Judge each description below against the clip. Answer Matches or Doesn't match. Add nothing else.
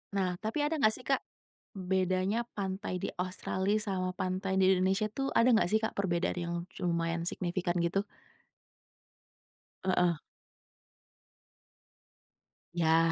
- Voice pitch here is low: Doesn't match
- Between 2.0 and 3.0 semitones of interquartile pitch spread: Matches